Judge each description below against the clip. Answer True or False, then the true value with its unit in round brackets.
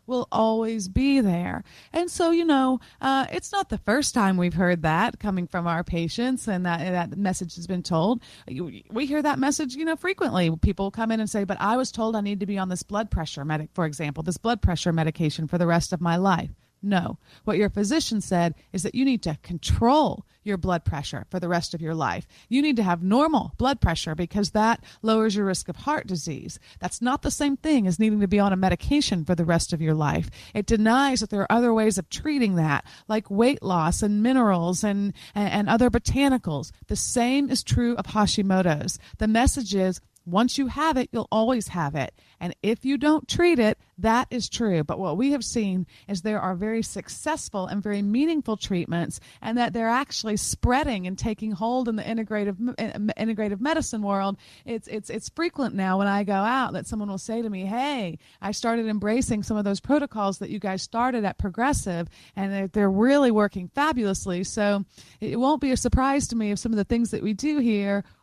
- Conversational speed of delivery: False (215 wpm)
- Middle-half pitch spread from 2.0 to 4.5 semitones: False (4.9 semitones)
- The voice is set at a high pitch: True (210 Hz)